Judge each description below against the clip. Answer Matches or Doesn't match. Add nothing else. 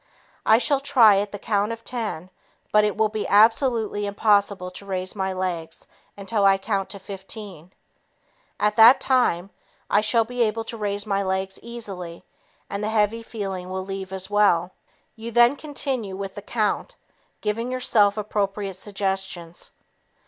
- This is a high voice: Matches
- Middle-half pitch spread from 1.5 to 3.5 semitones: Matches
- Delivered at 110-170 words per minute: Matches